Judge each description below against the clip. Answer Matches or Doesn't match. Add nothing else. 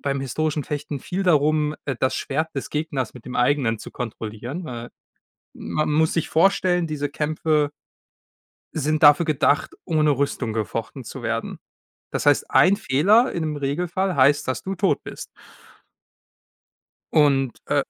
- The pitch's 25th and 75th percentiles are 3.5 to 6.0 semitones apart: Doesn't match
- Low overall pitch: Doesn't match